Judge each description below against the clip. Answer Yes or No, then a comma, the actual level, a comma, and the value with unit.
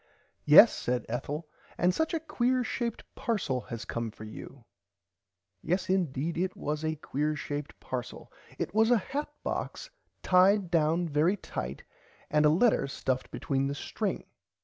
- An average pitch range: No, wide, 6.5 semitones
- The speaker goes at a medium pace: Yes, average, 150 wpm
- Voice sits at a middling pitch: Yes, medium, 160 Hz